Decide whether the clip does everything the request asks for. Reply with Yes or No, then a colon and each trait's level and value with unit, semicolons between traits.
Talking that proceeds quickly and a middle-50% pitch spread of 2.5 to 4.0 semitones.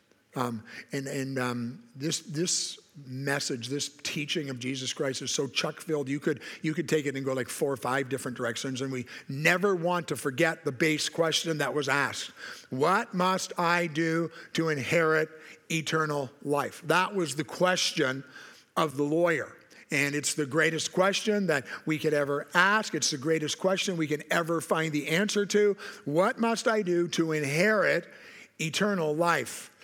No: average, 175 wpm; average, 3.4 semitones